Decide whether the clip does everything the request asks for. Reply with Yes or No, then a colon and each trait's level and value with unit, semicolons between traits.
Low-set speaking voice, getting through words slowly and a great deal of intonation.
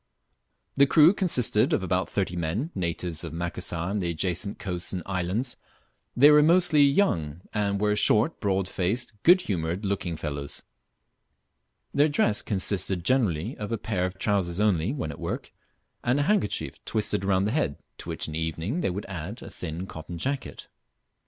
No: low, 100 Hz; average, 170 wpm; wide, 5.7 semitones